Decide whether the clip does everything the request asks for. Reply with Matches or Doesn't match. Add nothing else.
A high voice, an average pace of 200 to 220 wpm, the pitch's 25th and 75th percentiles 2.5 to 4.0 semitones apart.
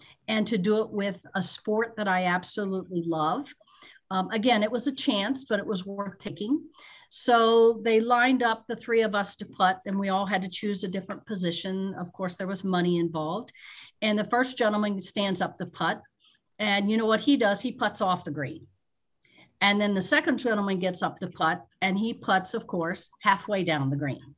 Matches